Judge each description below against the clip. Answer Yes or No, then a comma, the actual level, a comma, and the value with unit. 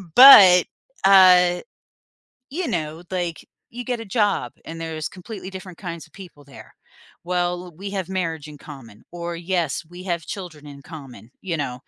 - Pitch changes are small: No, average, 3.1 semitones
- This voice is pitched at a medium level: Yes, medium, 175 Hz